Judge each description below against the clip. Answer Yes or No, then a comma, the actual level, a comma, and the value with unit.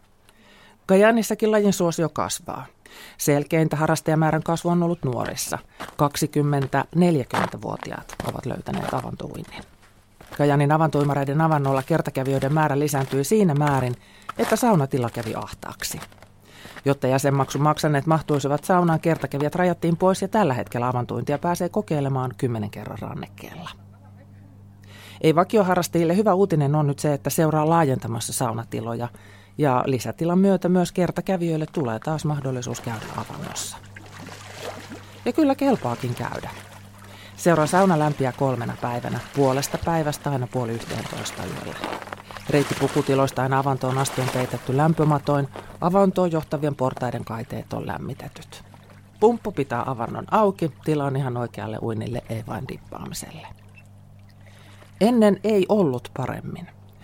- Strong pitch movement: Yes, wide, 5.8 semitones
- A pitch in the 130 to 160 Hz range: Yes, medium, 140 Hz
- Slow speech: No, average, 115 wpm